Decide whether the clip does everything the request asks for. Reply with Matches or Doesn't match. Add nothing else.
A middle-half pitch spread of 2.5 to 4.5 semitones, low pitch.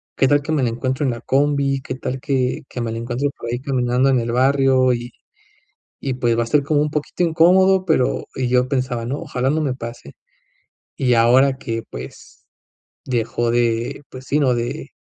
Matches